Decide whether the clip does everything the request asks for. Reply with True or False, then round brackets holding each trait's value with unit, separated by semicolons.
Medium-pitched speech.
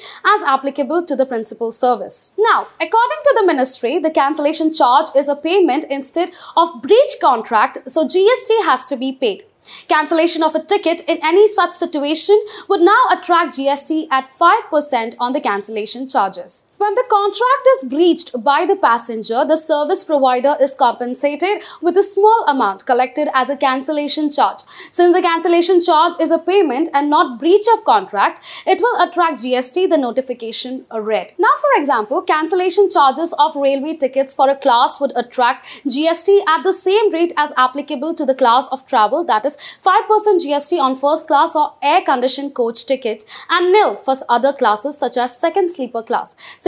False (300 Hz)